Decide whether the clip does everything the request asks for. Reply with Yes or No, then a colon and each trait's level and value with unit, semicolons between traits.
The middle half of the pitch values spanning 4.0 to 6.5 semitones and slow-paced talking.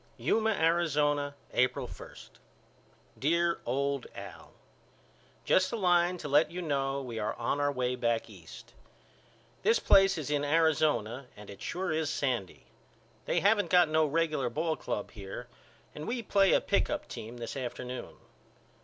No: average, 5.2 semitones; average, 155 wpm